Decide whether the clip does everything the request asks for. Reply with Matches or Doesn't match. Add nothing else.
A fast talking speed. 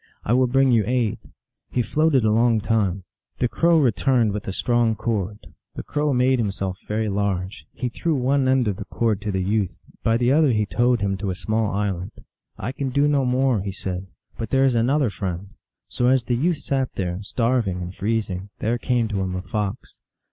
Matches